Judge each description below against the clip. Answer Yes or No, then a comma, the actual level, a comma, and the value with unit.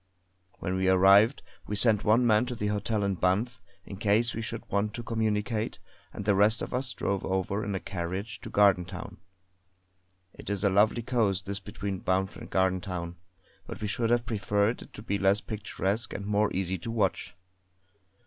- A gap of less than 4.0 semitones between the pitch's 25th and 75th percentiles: Yes, narrow, 2.5 semitones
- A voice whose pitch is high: No, low, 100 Hz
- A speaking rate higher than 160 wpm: Yes, average, 185 wpm